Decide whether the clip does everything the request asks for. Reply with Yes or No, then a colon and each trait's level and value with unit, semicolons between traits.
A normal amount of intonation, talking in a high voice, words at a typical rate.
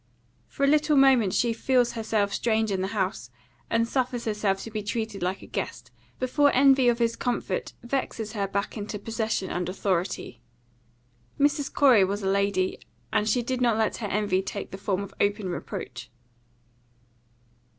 Yes: average, 3.7 semitones; high, 220 Hz; average, 170 wpm